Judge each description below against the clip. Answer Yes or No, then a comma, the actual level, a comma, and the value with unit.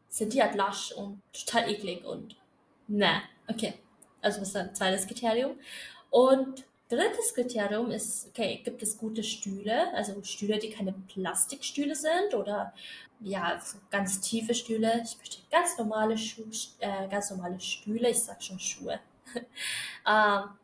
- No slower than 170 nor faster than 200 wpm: No, average, 150 wpm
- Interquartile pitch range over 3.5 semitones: No, average, 3.0 semitones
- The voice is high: Yes, high, 220 Hz